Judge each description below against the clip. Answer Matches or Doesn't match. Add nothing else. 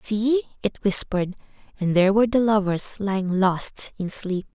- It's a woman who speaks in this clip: Matches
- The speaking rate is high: Doesn't match